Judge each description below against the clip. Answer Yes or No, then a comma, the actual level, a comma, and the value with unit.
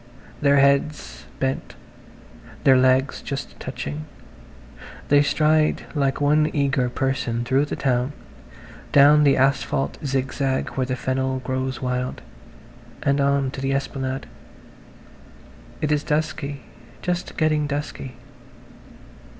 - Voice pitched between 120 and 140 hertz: Yes, low, 135 Hz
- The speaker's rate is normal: No, slow, 110 wpm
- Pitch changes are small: Yes, narrow, 1.7 semitones